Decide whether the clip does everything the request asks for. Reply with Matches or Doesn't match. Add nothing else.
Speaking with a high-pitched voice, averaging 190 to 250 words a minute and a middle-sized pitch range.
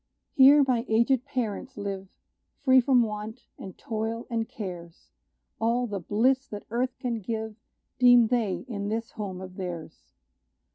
Doesn't match